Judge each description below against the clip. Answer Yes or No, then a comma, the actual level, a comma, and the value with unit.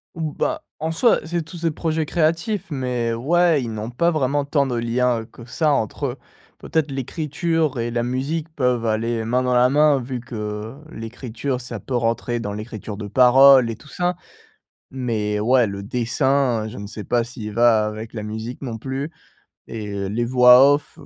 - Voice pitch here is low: Yes, low, 125 Hz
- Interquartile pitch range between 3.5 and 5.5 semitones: Yes, average, 4.1 semitones